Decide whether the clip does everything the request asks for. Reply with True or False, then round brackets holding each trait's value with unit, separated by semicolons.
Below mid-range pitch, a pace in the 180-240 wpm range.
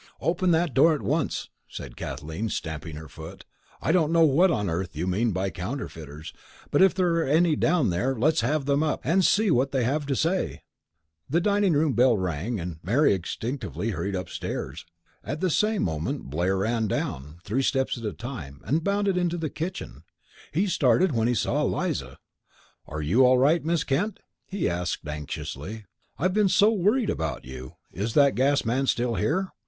True (130 Hz; 185 wpm)